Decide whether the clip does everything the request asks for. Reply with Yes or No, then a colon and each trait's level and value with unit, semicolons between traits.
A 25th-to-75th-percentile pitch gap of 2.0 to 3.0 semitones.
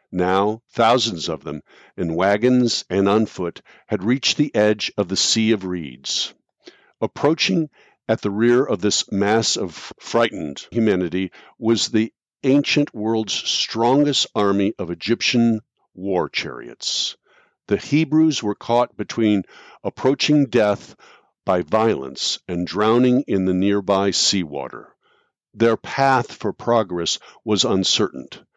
No: average, 4.0 semitones